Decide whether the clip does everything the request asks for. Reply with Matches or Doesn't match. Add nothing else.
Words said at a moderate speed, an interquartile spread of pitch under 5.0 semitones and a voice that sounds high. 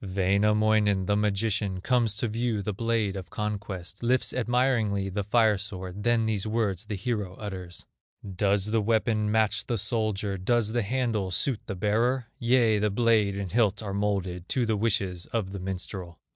Doesn't match